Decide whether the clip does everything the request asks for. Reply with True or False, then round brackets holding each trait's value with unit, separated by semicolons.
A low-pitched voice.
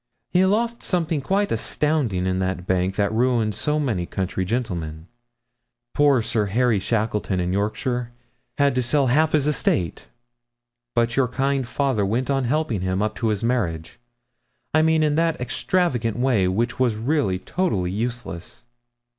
True (120 Hz)